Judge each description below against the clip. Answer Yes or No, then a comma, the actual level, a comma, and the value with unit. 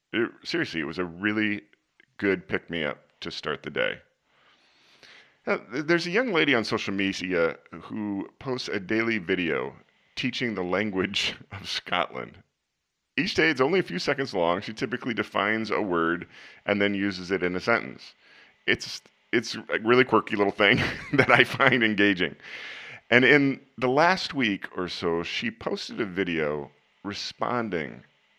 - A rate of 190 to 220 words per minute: No, average, 160 wpm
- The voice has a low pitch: Yes, low, 100 Hz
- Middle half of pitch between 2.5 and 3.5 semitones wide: No, average, 4.8 semitones